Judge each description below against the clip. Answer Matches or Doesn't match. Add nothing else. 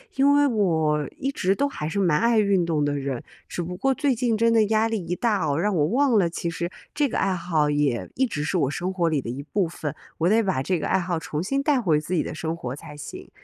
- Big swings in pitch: Matches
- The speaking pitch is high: Doesn't match